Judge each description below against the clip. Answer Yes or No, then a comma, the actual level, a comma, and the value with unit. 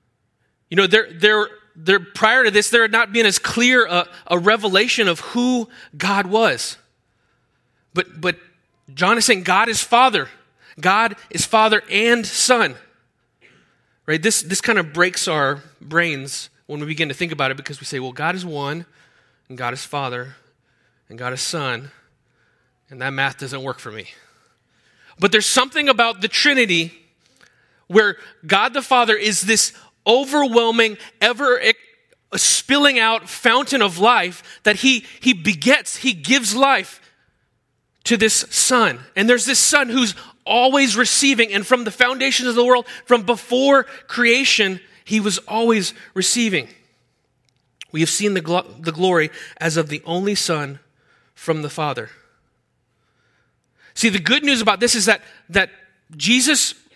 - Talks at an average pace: Yes, average, 155 wpm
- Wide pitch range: Yes, wide, 7.4 semitones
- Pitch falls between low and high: No, high, 205 Hz